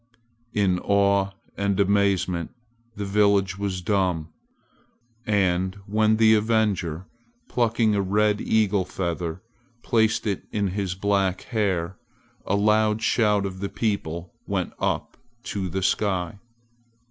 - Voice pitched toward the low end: Yes, low, 100 Hz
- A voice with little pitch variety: Yes, narrow, 2.2 semitones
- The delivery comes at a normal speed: No, slow, 120 wpm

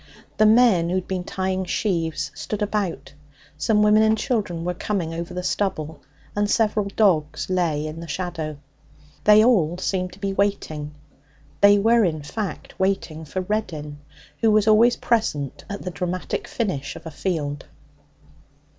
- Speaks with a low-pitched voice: No, medium, 185 Hz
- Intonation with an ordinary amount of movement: Yes, average, 4.5 semitones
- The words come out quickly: No, average, 155 wpm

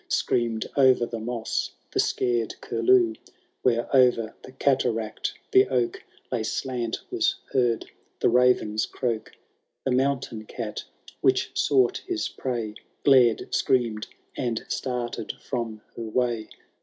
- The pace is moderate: No, slow, 120 wpm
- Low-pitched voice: Yes, low, 120 Hz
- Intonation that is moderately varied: No, narrow, 2.1 semitones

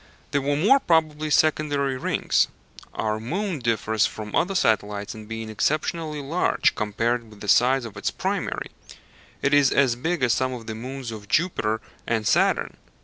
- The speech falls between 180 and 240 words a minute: No, average, 165 wpm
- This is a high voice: No, low, 125 Hz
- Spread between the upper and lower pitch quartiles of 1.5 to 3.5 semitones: No, wide, 5.5 semitones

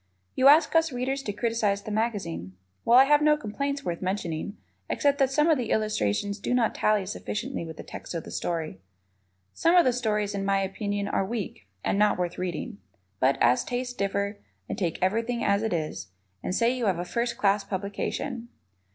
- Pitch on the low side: No, high, 210 Hz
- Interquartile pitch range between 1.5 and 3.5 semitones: No, average, 4.7 semitones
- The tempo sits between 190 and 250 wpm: Yes, average, 195 wpm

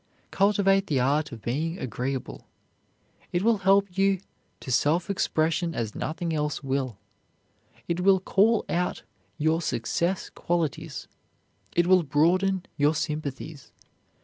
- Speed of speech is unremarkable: No, slow, 120 wpm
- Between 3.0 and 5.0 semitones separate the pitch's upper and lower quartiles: Yes, average, 4.7 semitones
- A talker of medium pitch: Yes, medium, 165 Hz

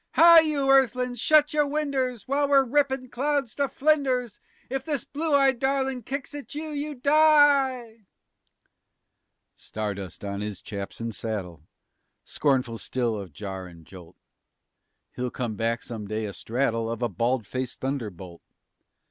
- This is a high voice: Yes, high, 235 Hz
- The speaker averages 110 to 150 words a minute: Yes, average, 145 wpm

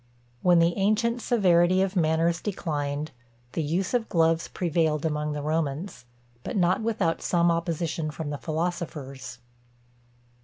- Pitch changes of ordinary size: Yes, average, 3.0 semitones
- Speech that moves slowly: Yes, slow, 130 wpm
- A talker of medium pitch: Yes, medium, 165 Hz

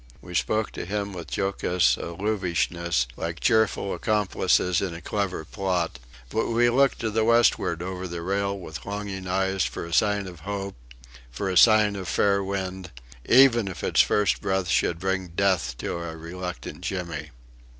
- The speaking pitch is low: Yes, very low, 95 Hz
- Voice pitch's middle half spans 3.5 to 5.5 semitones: No, average, 2.9 semitones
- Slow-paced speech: No, average, 165 wpm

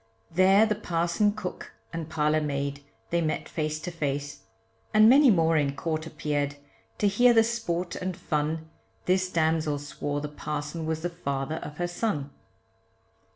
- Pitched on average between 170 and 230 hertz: No, medium, 160 Hz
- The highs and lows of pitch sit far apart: No, average, 3.6 semitones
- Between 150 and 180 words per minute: Yes, average, 155 wpm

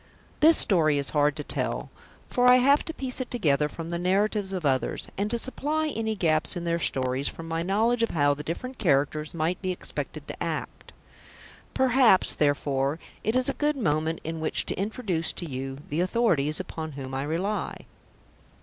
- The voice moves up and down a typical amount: No, wide, 7.1 semitones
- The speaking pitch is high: No, medium, 170 Hz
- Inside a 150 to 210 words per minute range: Yes, average, 185 wpm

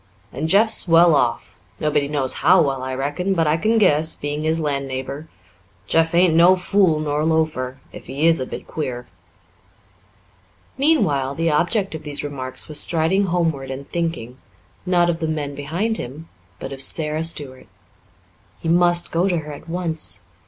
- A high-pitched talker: No, medium, 160 Hz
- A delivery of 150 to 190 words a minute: Yes, average, 170 wpm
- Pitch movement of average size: Yes, average, 3.5 semitones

